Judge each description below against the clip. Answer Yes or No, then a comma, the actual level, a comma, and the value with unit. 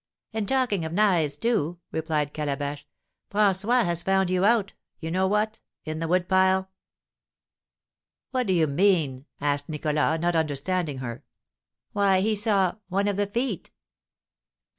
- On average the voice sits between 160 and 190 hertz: Yes, medium, 185 Hz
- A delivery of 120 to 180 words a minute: Yes, average, 140 wpm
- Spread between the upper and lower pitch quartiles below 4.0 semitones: No, average, 4.7 semitones